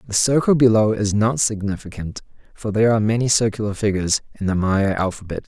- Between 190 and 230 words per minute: No, average, 175 wpm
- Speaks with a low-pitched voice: Yes, low, 105 Hz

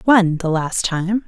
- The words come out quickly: No, average, 190 wpm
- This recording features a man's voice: No, female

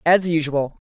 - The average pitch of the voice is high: No, medium, 160 Hz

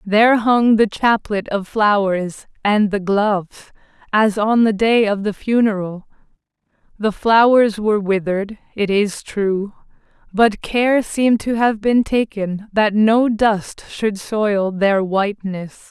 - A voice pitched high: Yes, high, 210 Hz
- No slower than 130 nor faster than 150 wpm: Yes, average, 140 wpm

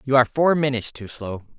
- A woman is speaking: No, male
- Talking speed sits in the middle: No, fast, 230 wpm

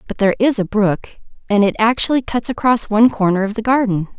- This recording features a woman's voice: Yes, female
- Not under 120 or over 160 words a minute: No, average, 200 wpm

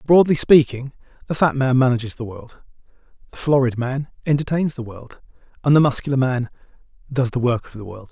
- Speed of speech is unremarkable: Yes, average, 180 wpm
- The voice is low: Yes, low, 130 Hz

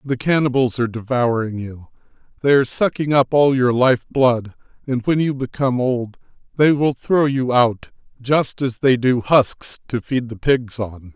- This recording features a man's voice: Yes, male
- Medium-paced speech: Yes, average, 175 wpm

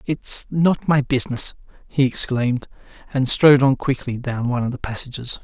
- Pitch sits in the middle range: No, low, 130 Hz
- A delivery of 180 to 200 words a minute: No, average, 165 wpm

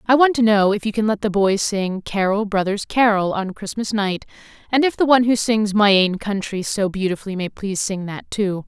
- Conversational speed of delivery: No, fast, 230 wpm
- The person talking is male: No, female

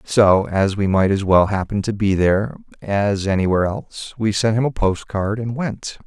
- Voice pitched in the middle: No, low, 105 Hz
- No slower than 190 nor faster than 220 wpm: Yes, average, 200 wpm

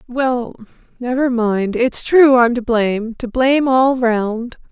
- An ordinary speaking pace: Yes, average, 155 wpm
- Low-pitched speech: No, high, 245 Hz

